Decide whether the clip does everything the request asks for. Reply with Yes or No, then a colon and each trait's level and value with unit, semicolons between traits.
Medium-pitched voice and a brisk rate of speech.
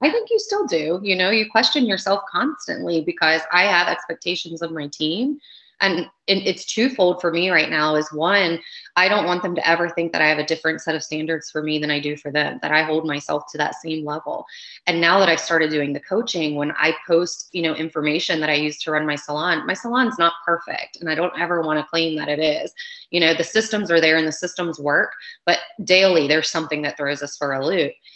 Yes: medium, 165 Hz; fast, 240 wpm